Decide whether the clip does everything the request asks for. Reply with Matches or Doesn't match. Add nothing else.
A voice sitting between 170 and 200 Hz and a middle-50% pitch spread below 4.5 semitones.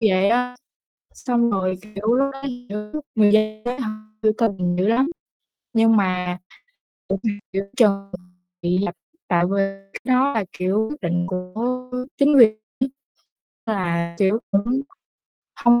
Doesn't match